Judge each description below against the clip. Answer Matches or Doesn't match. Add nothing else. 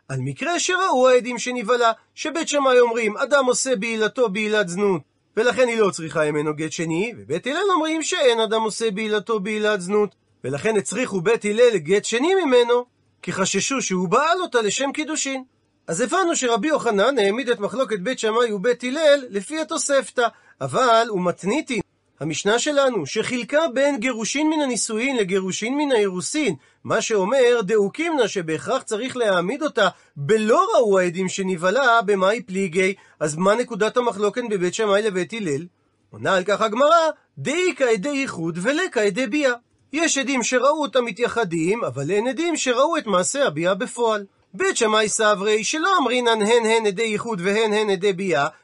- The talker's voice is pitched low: Doesn't match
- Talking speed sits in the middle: Doesn't match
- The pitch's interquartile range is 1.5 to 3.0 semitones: Doesn't match